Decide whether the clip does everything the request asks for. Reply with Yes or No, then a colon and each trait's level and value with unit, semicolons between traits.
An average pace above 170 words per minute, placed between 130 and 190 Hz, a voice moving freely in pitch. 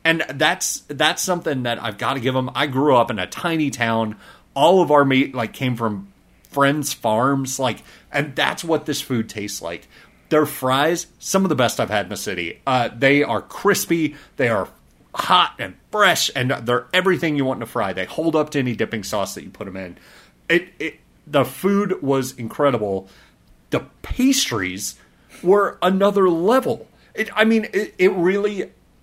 Yes: average, 190 wpm; medium, 140 Hz; wide, 6.9 semitones